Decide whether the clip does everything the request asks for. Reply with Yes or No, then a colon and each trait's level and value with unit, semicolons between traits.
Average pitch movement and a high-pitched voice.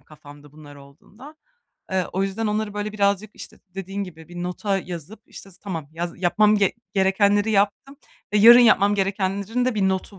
Yes: average, 3.0 semitones; high, 195 Hz